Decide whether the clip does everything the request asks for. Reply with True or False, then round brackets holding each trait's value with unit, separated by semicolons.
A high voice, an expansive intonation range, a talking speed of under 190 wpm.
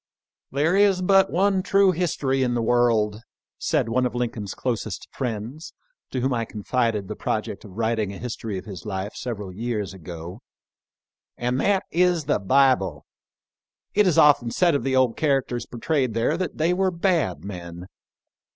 False (120 Hz; 6.9 semitones; 170 wpm)